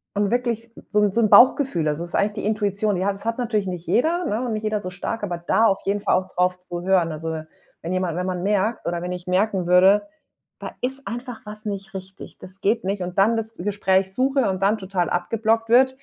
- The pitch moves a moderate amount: Yes, average, 3.5 semitones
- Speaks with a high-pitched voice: Yes, high, 200 Hz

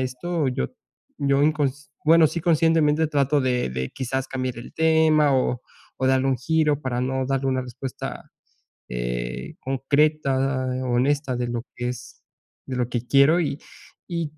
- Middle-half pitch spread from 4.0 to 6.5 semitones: No, average, 3.3 semitones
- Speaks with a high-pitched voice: No, low, 135 Hz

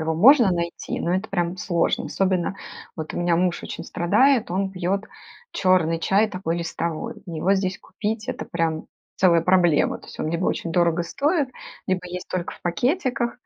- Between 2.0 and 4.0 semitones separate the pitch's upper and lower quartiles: Yes, average, 2.8 semitones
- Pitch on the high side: No, medium, 180 Hz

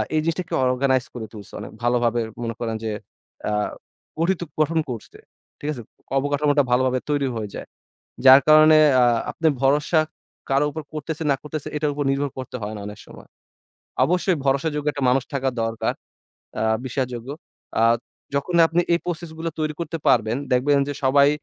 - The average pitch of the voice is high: No, medium, 140 Hz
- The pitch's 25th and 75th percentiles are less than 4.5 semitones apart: Yes, average, 3.6 semitones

